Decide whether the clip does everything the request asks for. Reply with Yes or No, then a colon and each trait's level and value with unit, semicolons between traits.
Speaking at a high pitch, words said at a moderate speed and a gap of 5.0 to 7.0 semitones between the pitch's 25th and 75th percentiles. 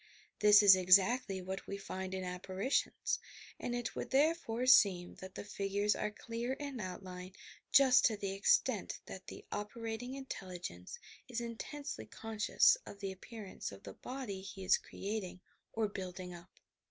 No: high, 200 Hz; average, 155 wpm; average, 3.8 semitones